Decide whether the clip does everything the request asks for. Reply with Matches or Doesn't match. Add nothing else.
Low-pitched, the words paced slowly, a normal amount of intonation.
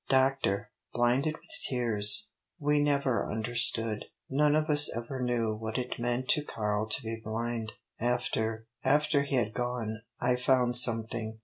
Doesn't match